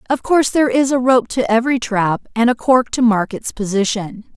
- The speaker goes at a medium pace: No, fast, 220 wpm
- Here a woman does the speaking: Yes, female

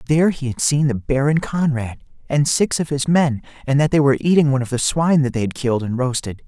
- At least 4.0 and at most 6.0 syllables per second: No, 6.2 syllables/s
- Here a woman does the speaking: No, male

